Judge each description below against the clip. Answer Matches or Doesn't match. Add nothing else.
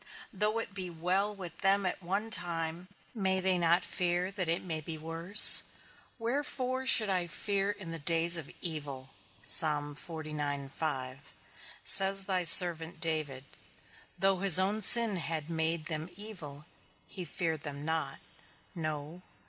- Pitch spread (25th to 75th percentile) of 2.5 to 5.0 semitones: Matches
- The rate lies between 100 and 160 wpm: Matches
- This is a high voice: Doesn't match